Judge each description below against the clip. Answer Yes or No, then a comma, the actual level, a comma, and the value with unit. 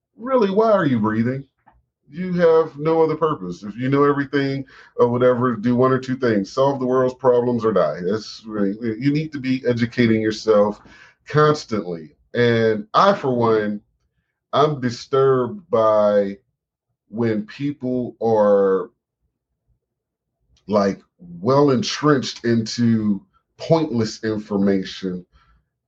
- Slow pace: Yes, slow, 120 wpm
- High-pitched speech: No, low, 120 Hz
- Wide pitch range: No, average, 4.8 semitones